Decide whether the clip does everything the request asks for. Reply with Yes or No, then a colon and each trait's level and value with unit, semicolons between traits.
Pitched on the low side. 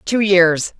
No: medium, 185 Hz